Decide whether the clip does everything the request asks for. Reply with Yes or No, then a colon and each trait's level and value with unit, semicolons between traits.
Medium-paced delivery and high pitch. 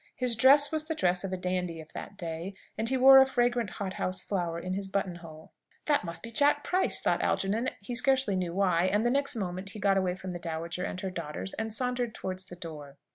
No: fast, 235 wpm; high, 195 Hz